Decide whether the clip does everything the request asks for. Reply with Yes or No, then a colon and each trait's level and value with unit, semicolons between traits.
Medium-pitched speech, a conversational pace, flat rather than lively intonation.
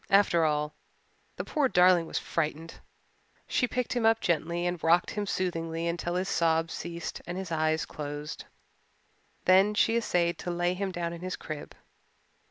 Yes: medium, 175 Hz; average, 165 wpm; narrow, 2.2 semitones